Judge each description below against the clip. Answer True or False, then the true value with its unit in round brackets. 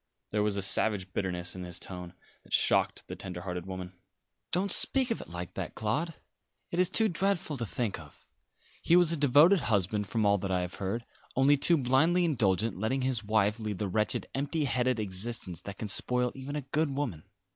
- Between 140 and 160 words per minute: False (200 wpm)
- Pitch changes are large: True (7.2 semitones)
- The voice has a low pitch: True (110 Hz)